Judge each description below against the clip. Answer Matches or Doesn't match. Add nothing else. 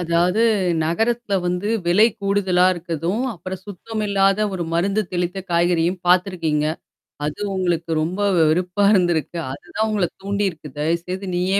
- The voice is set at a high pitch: Doesn't match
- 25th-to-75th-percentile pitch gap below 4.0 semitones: Matches